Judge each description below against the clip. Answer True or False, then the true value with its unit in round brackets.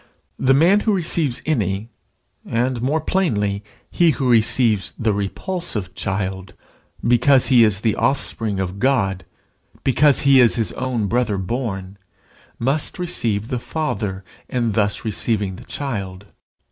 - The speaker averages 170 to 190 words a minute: False (135 wpm)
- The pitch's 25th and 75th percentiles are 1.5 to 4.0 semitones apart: False (5.1 semitones)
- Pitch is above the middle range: False (115 Hz)